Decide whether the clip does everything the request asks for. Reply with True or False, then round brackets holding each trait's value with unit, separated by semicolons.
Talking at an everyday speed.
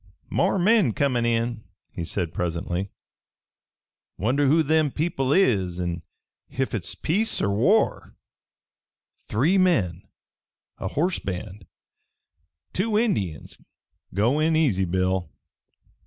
False (110 wpm)